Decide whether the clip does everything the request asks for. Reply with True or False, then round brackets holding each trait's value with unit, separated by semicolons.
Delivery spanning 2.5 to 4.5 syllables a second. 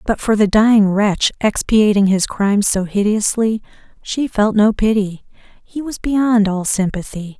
True (4.4 syllables/s)